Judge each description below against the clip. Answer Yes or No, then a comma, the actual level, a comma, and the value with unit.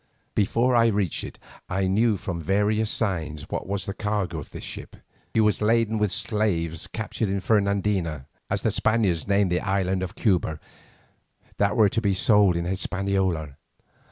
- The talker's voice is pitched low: Yes, low, 100 Hz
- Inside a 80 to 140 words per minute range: No, average, 165 wpm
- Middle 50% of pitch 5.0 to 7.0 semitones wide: No, average, 2.9 semitones